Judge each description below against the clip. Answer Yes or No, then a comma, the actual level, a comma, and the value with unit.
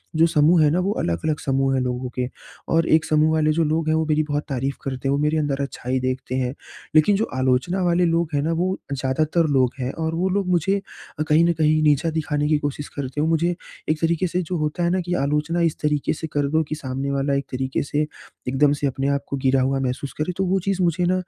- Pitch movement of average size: Yes, average, 3.5 semitones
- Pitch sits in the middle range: Yes, medium, 150 Hz